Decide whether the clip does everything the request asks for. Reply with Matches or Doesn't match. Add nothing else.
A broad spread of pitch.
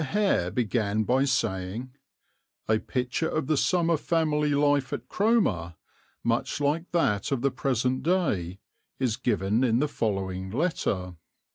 Matches